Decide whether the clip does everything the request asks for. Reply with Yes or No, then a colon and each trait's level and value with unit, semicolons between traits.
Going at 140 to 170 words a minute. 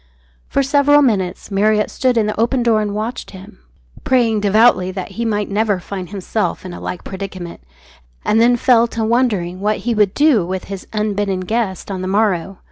No: average, 190 wpm